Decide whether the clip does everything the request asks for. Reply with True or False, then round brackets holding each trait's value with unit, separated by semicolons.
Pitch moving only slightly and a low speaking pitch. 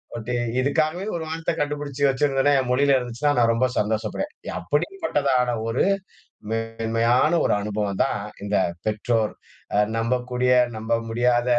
False (3.9 semitones; 125 Hz)